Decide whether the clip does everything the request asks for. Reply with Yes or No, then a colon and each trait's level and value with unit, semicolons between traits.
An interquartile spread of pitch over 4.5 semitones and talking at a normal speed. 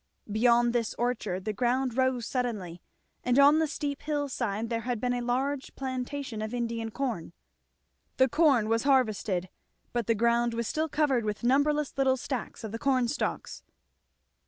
No: average, 2.9 semitones; average, 165 wpm